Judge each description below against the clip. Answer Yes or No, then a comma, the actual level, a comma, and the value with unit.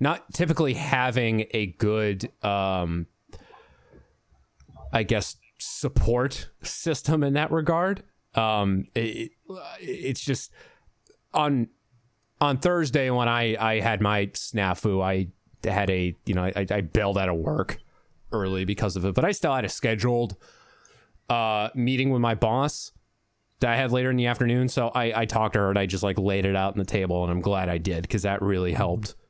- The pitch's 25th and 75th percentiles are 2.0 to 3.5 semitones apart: No, average, 4.4 semitones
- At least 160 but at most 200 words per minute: Yes, average, 170 wpm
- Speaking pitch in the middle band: No, low, 110 Hz